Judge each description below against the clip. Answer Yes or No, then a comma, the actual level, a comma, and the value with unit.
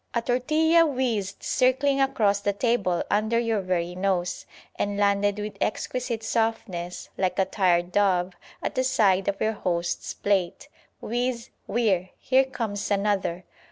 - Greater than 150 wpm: No, average, 140 wpm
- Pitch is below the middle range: No, high, 205 Hz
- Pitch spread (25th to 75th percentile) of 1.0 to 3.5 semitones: No, average, 4.3 semitones